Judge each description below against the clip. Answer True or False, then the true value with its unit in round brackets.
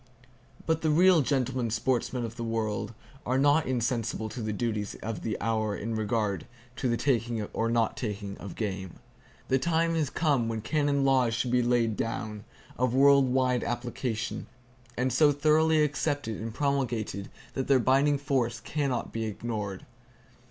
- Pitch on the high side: False (120 Hz)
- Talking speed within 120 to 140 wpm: False (165 wpm)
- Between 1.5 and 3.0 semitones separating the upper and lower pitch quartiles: False (3.8 semitones)